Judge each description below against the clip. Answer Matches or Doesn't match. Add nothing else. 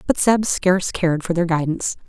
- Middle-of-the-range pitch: Matches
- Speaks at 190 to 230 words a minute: Matches